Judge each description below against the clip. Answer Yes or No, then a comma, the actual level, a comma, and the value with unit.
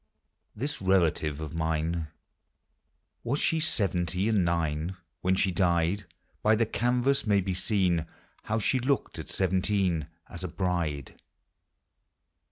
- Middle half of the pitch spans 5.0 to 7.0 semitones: No, average, 4.3 semitones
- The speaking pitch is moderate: No, very low, 95 Hz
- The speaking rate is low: Yes, slow, 125 wpm